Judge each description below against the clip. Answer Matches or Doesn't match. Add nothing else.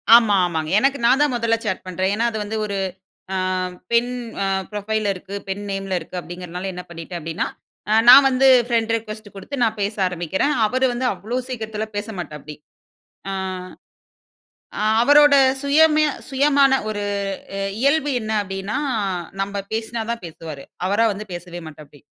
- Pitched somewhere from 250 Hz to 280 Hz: Doesn't match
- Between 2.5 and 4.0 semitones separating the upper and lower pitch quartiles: Doesn't match